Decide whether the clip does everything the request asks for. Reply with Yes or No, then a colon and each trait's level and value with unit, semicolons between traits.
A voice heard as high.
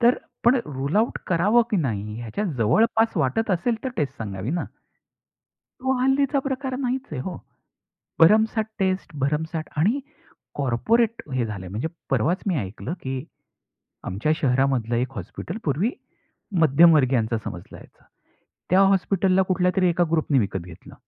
No: medium, 160 Hz